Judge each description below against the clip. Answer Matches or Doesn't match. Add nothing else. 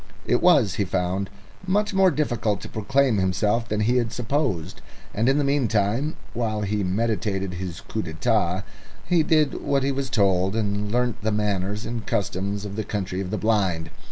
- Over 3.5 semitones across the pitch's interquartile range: Matches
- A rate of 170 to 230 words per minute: Matches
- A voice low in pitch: Matches